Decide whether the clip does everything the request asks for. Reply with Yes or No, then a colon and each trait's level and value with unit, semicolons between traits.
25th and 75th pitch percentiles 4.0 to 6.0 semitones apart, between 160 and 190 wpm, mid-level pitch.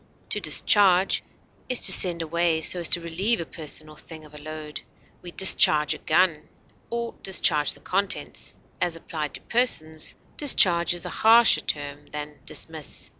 No: average, 3.6 semitones; average, 165 wpm; medium, 165 Hz